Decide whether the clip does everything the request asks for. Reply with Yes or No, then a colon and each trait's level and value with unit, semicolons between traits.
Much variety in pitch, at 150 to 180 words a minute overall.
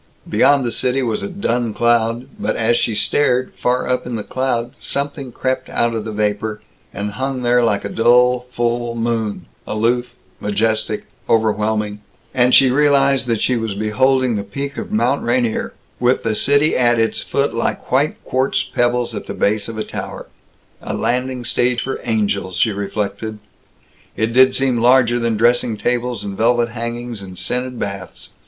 No: narrow, 2.5 semitones; average, 170 wpm